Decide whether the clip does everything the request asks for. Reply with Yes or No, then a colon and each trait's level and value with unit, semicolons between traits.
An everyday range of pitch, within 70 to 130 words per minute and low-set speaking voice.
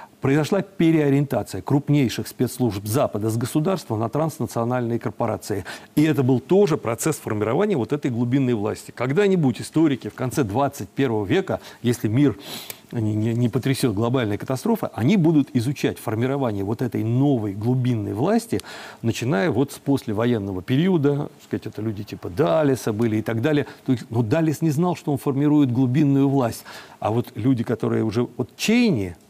No: average, 4.3 semitones; average, 145 wpm; low, 130 Hz